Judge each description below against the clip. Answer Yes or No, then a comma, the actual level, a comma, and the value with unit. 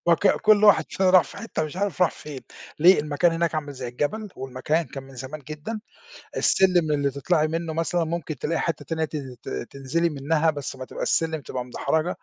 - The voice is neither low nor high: Yes, medium, 155 Hz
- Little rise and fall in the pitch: No, average, 3.4 semitones